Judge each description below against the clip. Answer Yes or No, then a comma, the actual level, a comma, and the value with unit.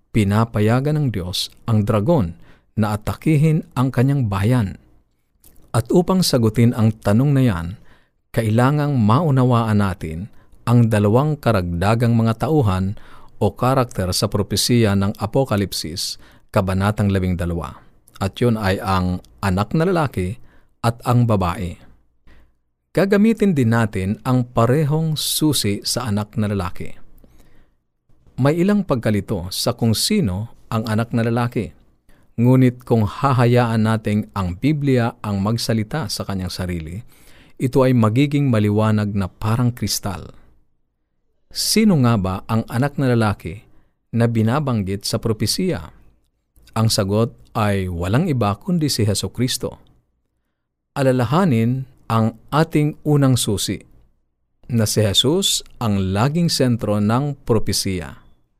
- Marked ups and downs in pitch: No, average, 4.4 semitones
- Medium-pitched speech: No, low, 110 Hz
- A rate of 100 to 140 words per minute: Yes, average, 115 wpm